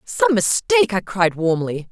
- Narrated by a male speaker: No, female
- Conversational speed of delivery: Yes, average, 155 wpm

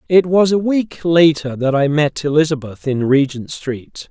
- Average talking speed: Yes, average, 175 wpm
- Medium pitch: Yes, medium, 150 Hz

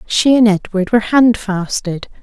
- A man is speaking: No, female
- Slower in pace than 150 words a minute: Yes, slow, 135 wpm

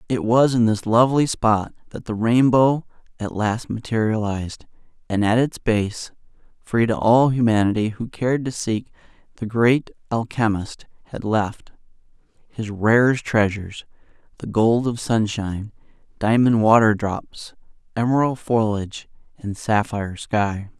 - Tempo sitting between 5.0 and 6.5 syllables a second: No, 4.4 syllables/s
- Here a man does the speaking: Yes, male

